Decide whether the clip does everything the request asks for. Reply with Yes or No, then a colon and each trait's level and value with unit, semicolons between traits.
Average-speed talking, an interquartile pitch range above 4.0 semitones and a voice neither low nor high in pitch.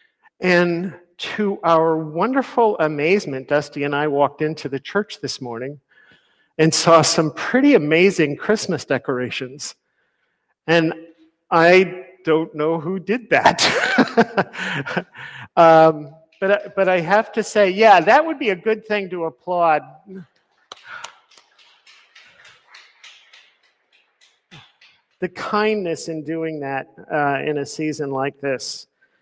No: slow, 115 wpm; average, 4.6 semitones; medium, 165 Hz